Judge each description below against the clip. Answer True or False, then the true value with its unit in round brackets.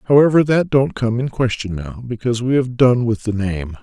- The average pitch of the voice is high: False (120 Hz)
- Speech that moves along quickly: True (220 wpm)